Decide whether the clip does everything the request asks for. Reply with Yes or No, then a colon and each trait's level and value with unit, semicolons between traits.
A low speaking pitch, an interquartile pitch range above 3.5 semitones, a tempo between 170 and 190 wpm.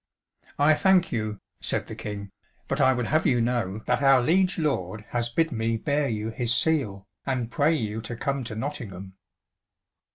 Yes: low, 120 Hz; average, 4.7 semitones; average, 175 wpm